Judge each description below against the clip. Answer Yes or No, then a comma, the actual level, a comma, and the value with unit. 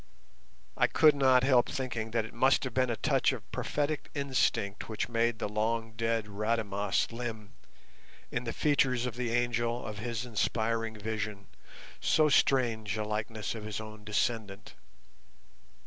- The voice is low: Yes, low, 115 Hz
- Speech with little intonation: Yes, narrow, 2.3 semitones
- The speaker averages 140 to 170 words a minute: Yes, average, 150 wpm